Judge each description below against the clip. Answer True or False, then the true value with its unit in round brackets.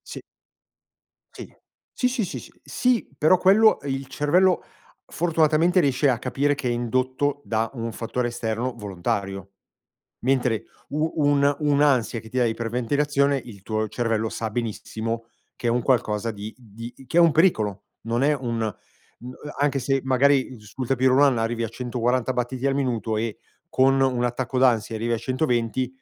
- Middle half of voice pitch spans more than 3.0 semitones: True (3.6 semitones)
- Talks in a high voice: False (125 Hz)